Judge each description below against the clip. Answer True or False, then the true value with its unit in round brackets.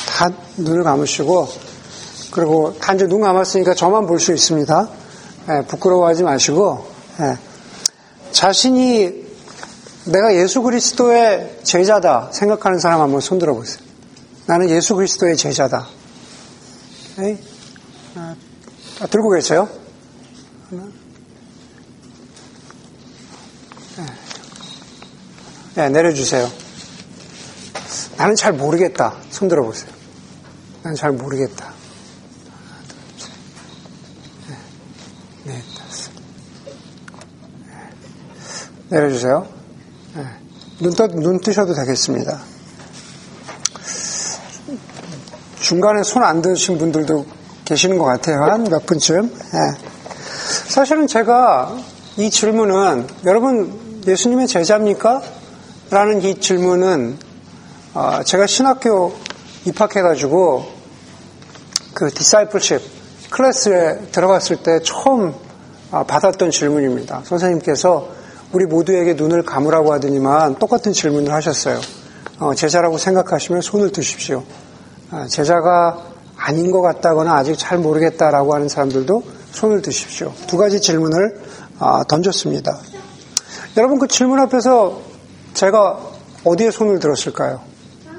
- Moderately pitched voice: True (180 Hz)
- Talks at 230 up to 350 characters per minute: False (215 characters per minute)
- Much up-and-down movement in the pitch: False (4.4 semitones)